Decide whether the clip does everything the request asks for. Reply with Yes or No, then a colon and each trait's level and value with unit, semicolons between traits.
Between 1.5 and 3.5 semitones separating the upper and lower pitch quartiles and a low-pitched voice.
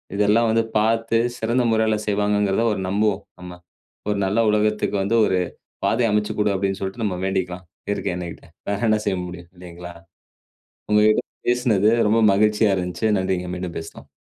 Yes: narrow, 2.6 semitones; low, 105 Hz